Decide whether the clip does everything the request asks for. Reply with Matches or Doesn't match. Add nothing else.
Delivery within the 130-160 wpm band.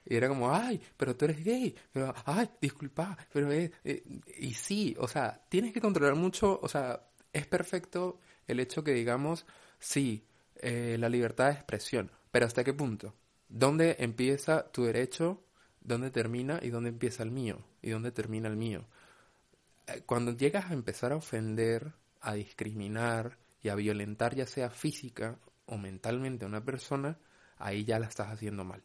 Doesn't match